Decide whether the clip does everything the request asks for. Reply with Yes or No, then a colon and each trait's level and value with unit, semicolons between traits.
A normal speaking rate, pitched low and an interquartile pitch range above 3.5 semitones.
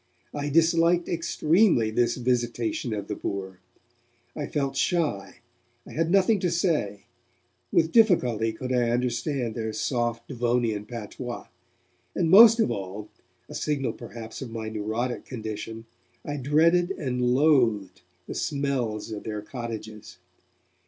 No: slow, 130 wpm; low, 120 Hz; wide, 5.4 semitones